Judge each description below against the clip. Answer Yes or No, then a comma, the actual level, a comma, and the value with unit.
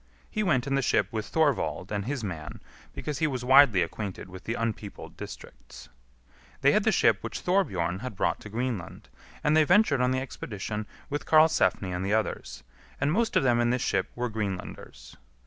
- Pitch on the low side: Yes, low, 120 Hz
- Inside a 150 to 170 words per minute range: No, average, 190 wpm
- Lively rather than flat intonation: Yes, wide, 6.0 semitones